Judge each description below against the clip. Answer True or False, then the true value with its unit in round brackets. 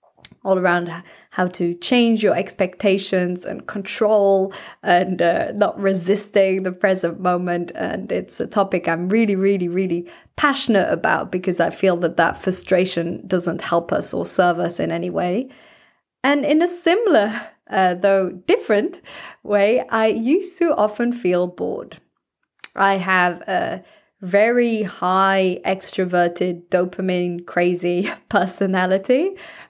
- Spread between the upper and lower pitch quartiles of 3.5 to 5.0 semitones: False (2.8 semitones)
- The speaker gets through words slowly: True (130 wpm)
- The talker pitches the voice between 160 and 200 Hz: True (190 Hz)